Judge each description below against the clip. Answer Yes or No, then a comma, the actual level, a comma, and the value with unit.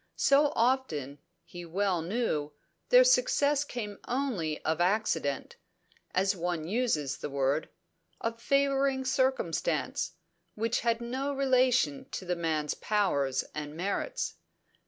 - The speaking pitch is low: No, high, 205 Hz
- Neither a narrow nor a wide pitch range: No, wide, 8.5 semitones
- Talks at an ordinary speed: No, slow, 115 wpm